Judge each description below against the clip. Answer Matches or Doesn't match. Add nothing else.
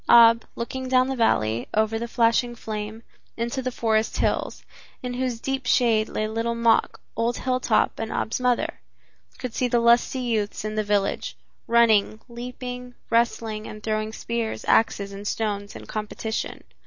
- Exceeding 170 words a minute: Doesn't match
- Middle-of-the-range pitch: Doesn't match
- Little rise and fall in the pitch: Matches